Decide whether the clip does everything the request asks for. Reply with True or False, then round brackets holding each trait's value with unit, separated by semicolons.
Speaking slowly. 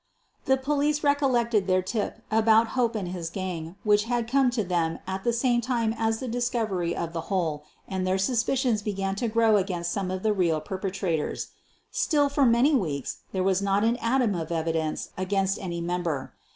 False (185 wpm)